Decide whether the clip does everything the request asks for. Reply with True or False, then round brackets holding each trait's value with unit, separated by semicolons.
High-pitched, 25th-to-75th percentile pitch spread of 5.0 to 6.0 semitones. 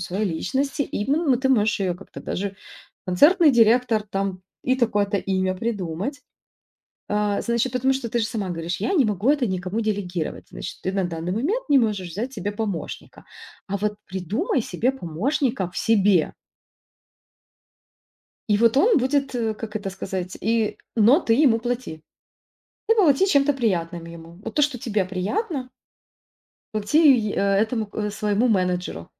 True (215 Hz; 5.3 semitones)